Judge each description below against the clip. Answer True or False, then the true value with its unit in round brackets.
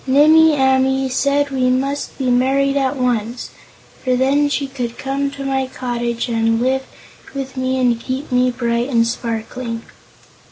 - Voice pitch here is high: True (260 Hz)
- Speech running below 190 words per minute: True (155 wpm)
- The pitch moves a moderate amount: False (2.2 semitones)